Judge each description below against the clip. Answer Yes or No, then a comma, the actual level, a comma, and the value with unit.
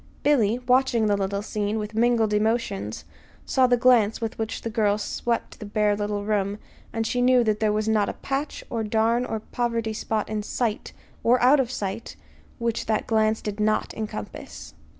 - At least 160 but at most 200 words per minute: Yes, average, 185 wpm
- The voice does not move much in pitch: Yes, narrow, 2.1 semitones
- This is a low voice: No, high, 220 Hz